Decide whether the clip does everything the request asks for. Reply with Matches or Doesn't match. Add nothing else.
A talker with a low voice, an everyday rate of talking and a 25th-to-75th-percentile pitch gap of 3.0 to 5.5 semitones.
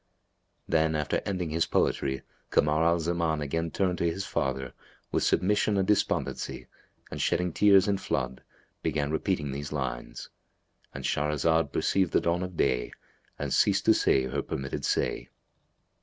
Matches